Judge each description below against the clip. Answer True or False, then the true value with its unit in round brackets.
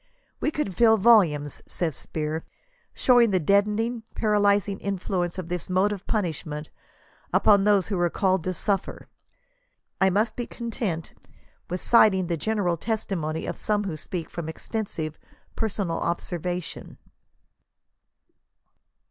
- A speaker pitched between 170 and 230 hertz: True (190 Hz)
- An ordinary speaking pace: False (125 wpm)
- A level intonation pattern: False (3.7 semitones)